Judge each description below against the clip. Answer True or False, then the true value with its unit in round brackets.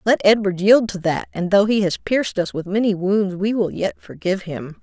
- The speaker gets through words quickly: True (235 wpm)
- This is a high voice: True (200 Hz)